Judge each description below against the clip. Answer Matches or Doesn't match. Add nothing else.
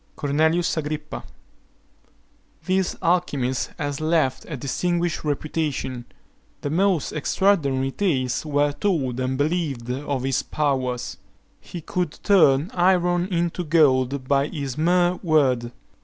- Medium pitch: Matches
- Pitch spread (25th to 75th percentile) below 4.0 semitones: Doesn't match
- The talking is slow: Matches